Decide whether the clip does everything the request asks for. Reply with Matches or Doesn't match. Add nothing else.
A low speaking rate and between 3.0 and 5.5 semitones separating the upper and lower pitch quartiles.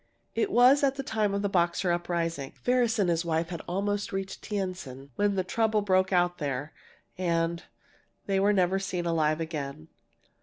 Doesn't match